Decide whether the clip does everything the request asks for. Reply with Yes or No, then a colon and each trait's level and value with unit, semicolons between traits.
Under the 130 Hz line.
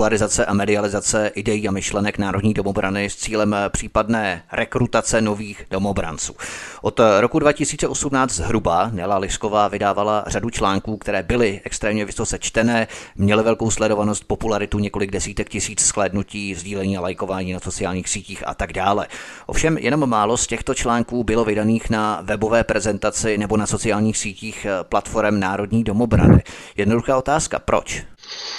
Yes: low, 105 Hz